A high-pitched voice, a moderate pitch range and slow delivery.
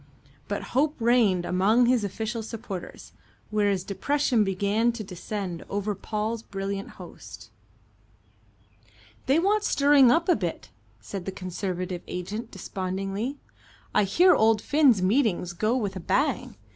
Yes: high, 210 Hz; average, 4.2 semitones; slow, 130 wpm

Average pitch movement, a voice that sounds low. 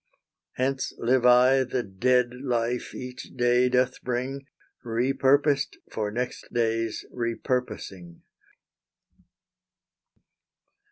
No: narrow, 1.7 semitones; low, 125 Hz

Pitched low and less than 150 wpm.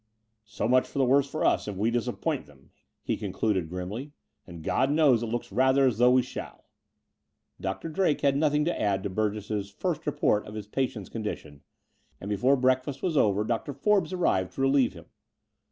No: low, 120 Hz; average, 200 wpm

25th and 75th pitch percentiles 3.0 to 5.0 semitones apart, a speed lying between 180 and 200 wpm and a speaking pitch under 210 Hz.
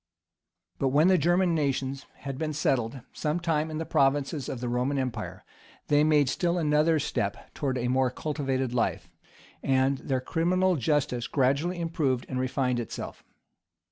No: average, 3.3 semitones; average, 160 wpm; medium, 140 Hz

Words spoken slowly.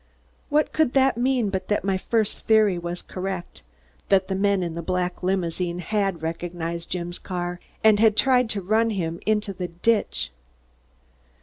No: average, 165 wpm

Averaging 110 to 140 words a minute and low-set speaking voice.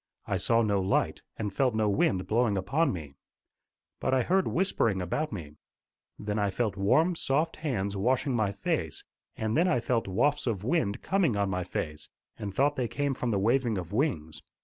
No: average, 190 wpm; low, 110 Hz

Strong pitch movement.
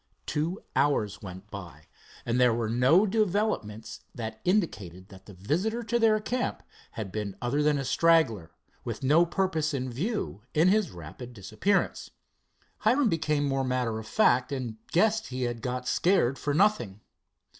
Yes: wide, 8.8 semitones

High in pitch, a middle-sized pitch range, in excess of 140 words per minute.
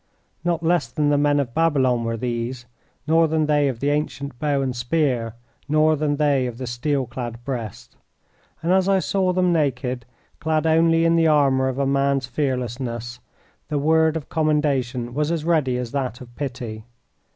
No: medium, 140 Hz; average, 3.9 semitones; average, 180 wpm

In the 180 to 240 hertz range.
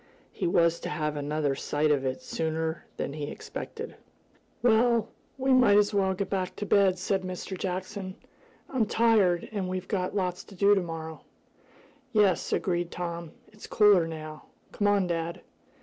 Yes: medium, 185 Hz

